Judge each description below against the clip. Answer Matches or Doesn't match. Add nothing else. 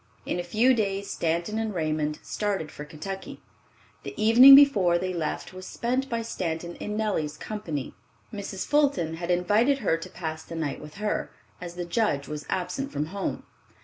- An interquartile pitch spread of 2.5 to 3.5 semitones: Doesn't match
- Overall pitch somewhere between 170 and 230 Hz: Matches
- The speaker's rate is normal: Matches